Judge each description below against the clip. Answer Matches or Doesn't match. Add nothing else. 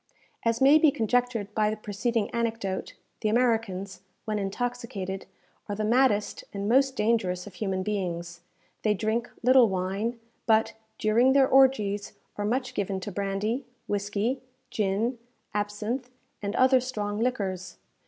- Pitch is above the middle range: Matches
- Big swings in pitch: Doesn't match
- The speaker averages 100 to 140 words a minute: Matches